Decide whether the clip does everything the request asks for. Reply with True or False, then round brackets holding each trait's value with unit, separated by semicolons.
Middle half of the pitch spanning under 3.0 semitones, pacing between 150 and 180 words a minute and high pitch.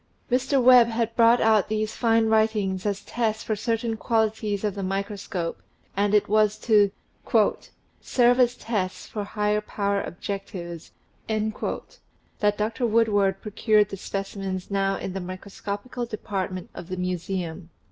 False (2.4 semitones; 140 wpm; 210 Hz)